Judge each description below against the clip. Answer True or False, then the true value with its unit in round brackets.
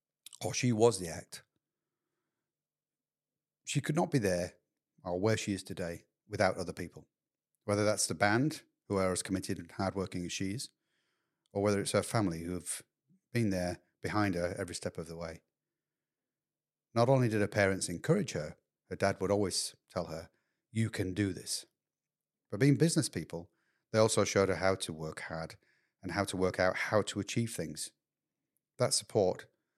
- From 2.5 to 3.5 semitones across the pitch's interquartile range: False (3.9 semitones)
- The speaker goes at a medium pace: True (175 wpm)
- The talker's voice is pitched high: False (100 Hz)